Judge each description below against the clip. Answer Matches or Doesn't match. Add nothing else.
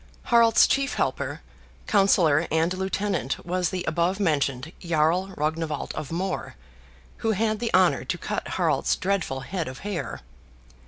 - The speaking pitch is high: Doesn't match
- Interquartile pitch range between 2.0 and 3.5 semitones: Doesn't match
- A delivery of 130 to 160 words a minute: Matches